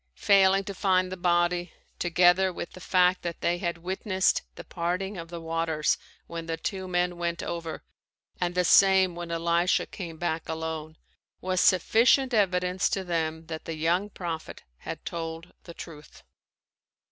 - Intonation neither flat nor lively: No, narrow, 2.0 semitones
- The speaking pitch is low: No, medium, 175 Hz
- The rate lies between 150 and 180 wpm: Yes, average, 160 wpm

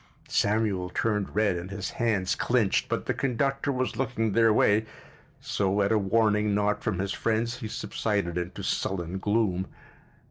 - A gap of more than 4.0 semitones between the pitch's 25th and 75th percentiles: No, average, 2.8 semitones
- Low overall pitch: Yes, low, 105 Hz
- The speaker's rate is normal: Yes, average, 155 wpm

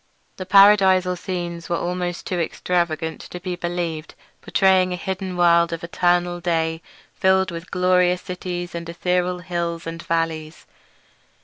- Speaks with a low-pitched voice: No, medium, 175 Hz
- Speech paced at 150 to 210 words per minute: No, slow, 135 wpm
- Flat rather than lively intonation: Yes, narrow, 1.3 semitones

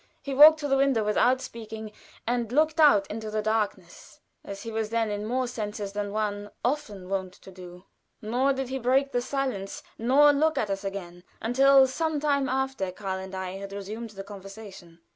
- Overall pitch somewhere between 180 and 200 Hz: No, high, 220 Hz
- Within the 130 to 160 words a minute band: No, average, 190 wpm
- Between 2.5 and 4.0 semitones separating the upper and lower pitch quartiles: No, average, 5.2 semitones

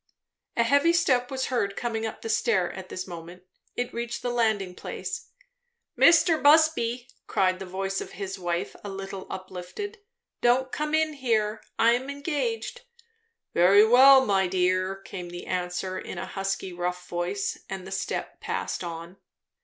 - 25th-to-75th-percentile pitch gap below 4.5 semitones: No, average, 5.3 semitones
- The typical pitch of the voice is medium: No, high, 200 Hz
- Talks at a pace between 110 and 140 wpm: No, average, 160 wpm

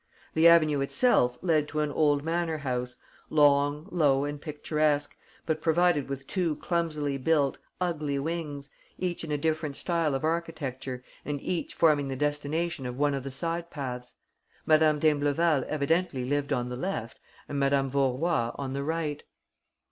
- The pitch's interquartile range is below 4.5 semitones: Yes, average, 2.9 semitones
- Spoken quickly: No, average, 155 wpm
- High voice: No, medium, 145 Hz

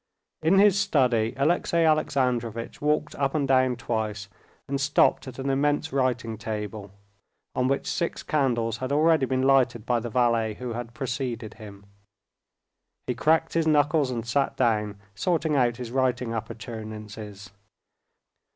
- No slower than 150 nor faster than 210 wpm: No, average, 140 wpm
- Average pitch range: Yes, average, 4.0 semitones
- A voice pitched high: No, low, 125 Hz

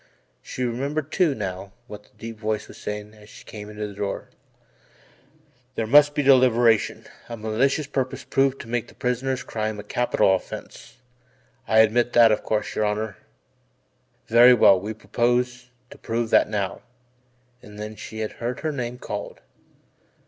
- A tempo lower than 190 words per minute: Yes, average, 165 wpm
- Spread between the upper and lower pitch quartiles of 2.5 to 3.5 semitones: Yes, average, 2.8 semitones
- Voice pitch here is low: Yes, low, 115 Hz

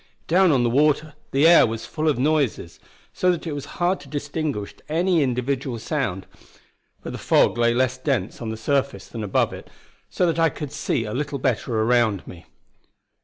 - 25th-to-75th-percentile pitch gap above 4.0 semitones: Yes, average, 4.7 semitones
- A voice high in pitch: No, low, 135 Hz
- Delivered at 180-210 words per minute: Yes, average, 190 wpm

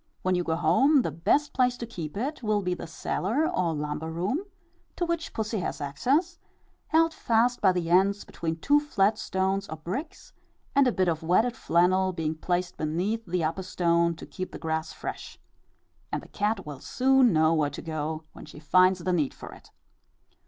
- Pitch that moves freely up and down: Yes, wide, 6.1 semitones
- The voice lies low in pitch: No, medium, 185 Hz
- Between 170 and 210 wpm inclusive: Yes, average, 190 wpm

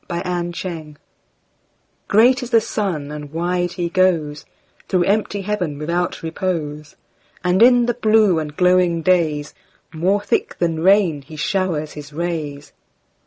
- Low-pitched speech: No, medium, 175 Hz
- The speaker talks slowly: Yes, slow, 120 wpm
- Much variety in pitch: No, average, 3.8 semitones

